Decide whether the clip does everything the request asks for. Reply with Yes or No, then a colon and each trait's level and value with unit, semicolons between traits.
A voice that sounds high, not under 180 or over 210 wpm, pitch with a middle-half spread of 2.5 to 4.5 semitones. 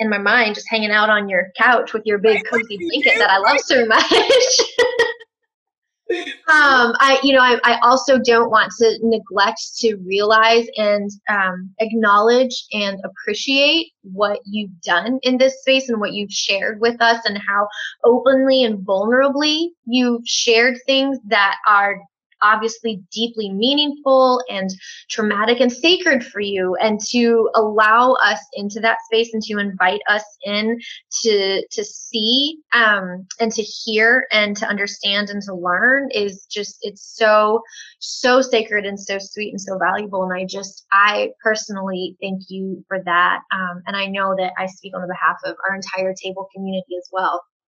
No: high, 215 Hz; average, 165 wpm; average, 3.7 semitones